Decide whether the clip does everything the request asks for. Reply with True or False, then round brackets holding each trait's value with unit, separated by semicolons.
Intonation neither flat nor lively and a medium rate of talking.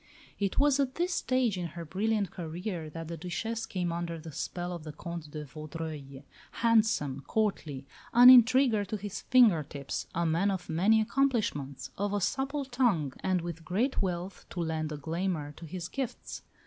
False (5.7 semitones; 175 wpm)